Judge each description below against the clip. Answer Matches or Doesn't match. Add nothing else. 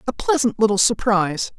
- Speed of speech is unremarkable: Matches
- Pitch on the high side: Matches